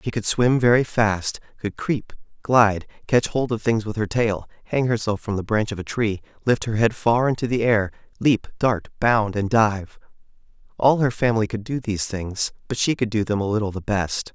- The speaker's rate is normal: No, fast, 215 wpm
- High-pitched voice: No, low, 110 Hz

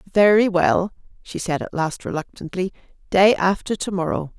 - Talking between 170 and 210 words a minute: No, average, 150 wpm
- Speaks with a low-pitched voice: No, medium, 185 Hz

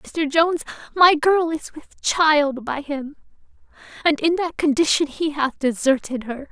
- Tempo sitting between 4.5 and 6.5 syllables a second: No, 4.2 syllables/s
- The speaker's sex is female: Yes, female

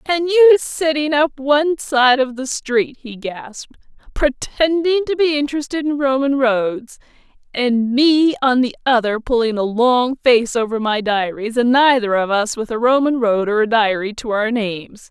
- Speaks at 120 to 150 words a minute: No, average, 175 wpm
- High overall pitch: Yes, very high, 255 Hz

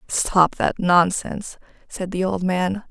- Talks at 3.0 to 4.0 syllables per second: Yes, 3.8 syllables/s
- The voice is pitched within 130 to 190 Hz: Yes, medium, 185 Hz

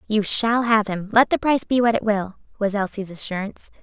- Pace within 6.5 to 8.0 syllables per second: No, 5.7 syllables/s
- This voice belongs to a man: No, female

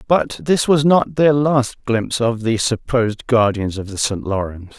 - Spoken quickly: No, average, 190 wpm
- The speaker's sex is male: Yes, male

